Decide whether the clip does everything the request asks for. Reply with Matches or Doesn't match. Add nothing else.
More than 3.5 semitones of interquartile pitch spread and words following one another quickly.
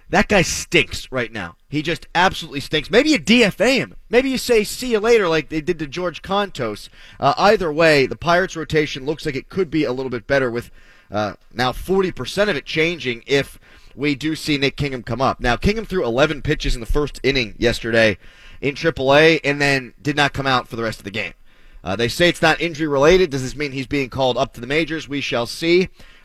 Matches